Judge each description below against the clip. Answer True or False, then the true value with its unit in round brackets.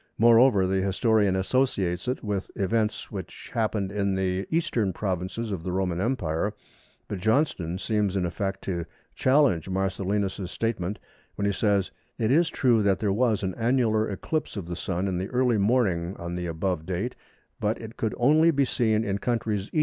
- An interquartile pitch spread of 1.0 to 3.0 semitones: False (3.6 semitones)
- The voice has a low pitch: True (100 Hz)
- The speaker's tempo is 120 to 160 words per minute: False (175 wpm)